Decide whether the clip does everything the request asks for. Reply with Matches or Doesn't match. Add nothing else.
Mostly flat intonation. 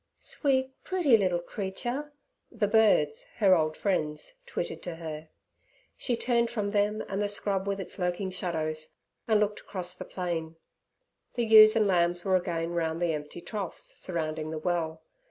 Doesn't match